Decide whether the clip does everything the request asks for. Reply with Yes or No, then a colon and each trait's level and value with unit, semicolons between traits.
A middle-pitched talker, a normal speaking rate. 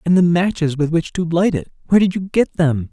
No: medium, 170 Hz; fast, 245 wpm